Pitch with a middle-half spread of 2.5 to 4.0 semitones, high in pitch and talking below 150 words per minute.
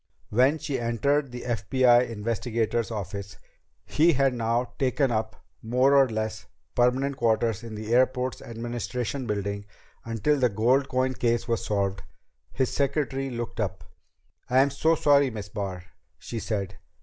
No: average, 3.3 semitones; low, 120 Hz; average, 140 wpm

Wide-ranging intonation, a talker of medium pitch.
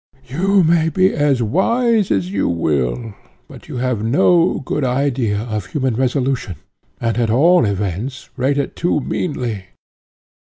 No: wide, 6.6 semitones; low, 130 Hz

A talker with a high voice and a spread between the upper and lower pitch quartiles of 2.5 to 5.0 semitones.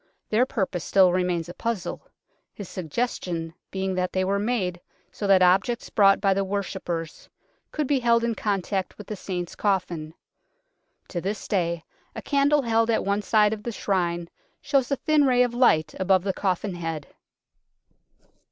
Yes: high, 195 Hz; average, 4.2 semitones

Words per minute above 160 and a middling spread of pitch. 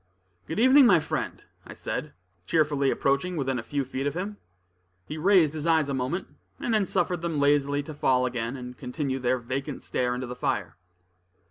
Yes: average, 190 wpm; average, 4.3 semitones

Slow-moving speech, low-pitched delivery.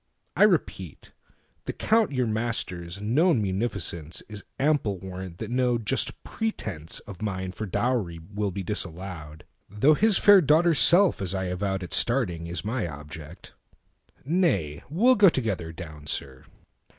Yes: slow, 125 wpm; low, 100 Hz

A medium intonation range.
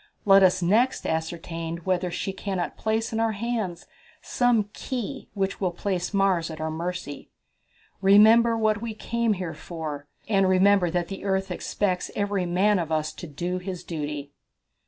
Yes: average, 3.5 semitones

